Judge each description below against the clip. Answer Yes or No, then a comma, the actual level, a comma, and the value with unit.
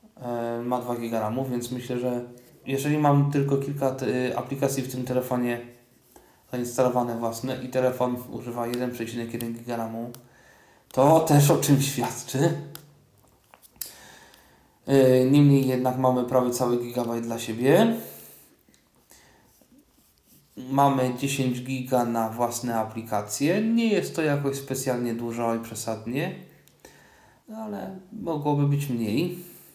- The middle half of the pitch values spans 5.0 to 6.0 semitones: No, narrow, 2.6 semitones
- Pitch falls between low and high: No, low, 125 Hz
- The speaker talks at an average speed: No, slow, 105 wpm